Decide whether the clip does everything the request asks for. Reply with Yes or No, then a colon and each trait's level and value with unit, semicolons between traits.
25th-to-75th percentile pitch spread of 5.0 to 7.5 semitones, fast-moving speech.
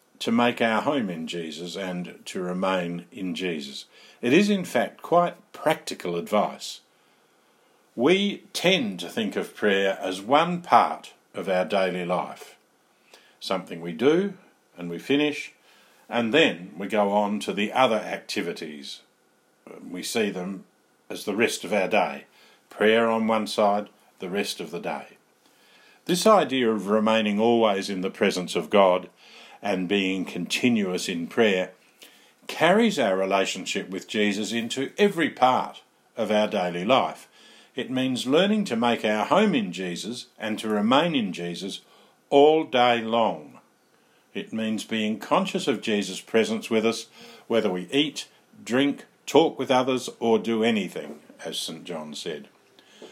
No: average, 5.3 semitones; average, 150 wpm